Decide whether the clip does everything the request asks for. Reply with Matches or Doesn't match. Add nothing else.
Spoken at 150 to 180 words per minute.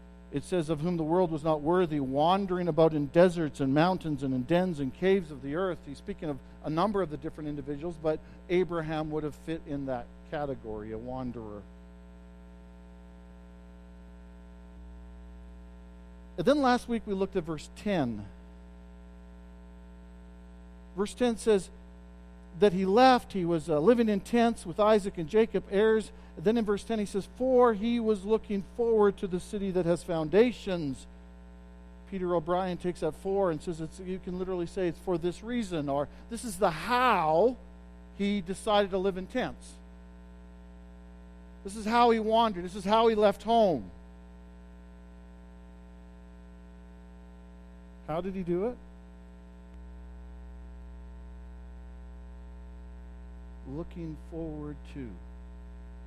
Doesn't match